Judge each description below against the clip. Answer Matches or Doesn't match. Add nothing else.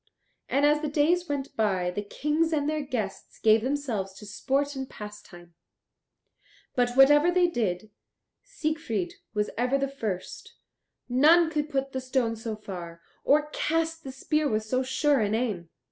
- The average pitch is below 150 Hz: Doesn't match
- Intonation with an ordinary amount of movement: Doesn't match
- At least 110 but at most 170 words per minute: Matches